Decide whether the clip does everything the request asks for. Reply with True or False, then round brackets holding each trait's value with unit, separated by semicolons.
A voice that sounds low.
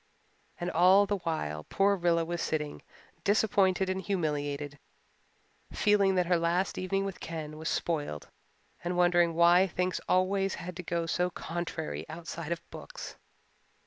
False (175 Hz)